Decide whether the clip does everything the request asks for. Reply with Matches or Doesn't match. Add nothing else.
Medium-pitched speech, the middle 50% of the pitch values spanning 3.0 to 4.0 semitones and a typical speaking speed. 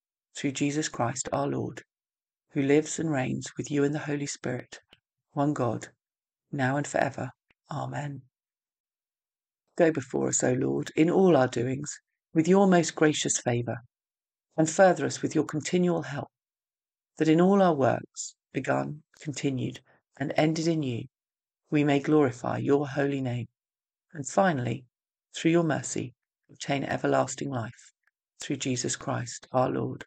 Matches